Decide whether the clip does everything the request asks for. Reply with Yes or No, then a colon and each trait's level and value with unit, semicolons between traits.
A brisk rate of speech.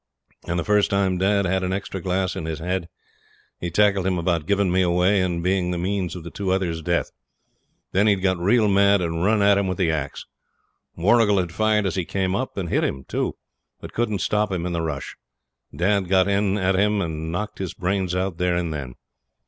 Yes: fast, 220 wpm